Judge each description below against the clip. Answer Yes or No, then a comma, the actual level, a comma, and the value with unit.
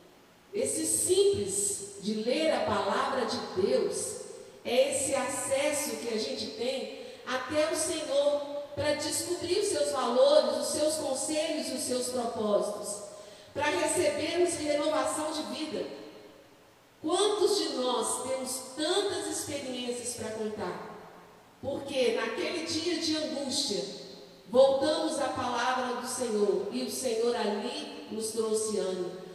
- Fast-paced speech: No, slow, 120 wpm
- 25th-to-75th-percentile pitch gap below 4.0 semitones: No, average, 5.1 semitones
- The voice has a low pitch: No, very high, 275 Hz